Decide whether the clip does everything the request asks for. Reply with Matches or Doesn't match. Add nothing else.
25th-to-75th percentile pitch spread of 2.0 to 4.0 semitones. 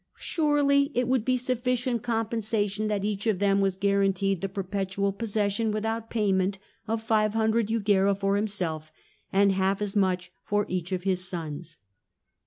Matches